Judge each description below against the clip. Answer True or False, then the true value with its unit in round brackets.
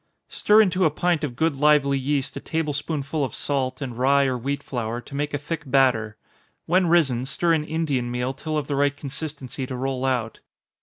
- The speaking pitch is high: False (140 Hz)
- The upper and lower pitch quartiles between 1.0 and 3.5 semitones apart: True (2.9 semitones)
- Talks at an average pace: False (210 wpm)